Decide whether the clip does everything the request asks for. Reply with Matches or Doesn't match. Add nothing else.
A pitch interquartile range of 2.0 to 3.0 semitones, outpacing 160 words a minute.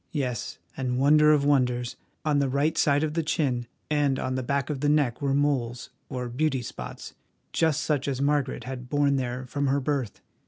Matches